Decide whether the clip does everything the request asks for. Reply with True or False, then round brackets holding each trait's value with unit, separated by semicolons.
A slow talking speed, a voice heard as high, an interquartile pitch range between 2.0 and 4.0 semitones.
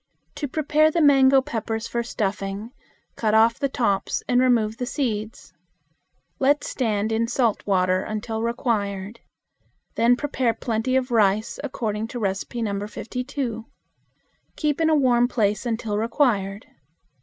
True (130 wpm; 230 Hz; 3.3 semitones)